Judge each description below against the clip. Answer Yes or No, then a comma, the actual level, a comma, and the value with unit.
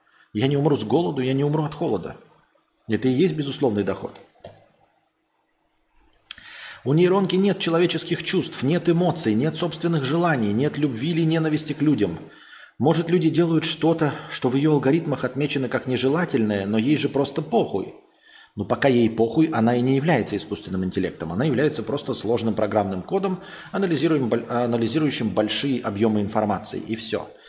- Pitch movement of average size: No, wide, 6.2 semitones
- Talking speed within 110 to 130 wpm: No, average, 150 wpm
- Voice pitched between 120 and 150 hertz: Yes, medium, 140 Hz